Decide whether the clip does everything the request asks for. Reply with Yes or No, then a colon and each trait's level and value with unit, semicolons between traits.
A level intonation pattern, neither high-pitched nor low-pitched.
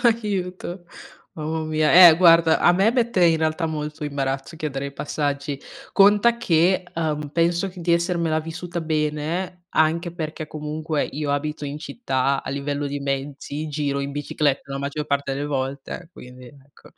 No: average, 3.2 semitones; medium, 155 Hz